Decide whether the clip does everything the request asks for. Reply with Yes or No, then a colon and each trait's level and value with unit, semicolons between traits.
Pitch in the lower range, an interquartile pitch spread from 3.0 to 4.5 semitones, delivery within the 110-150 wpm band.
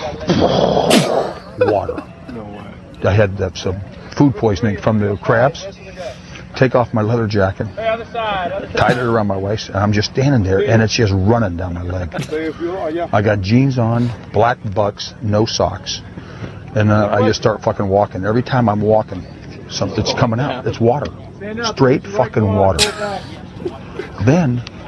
Yes: low, 110 Hz; average, 3.7 semitones; average, 140 wpm